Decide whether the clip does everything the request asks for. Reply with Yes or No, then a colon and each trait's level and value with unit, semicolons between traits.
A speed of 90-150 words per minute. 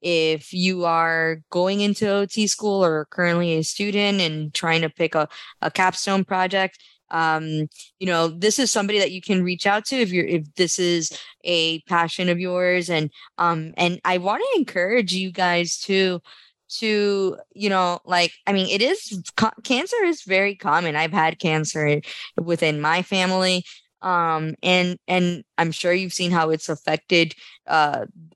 No: average, 170 wpm